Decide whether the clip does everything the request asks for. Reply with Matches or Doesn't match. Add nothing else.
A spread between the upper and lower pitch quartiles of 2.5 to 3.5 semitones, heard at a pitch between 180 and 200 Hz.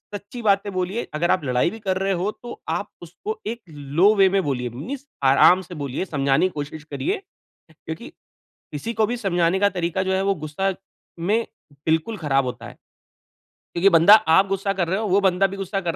Doesn't match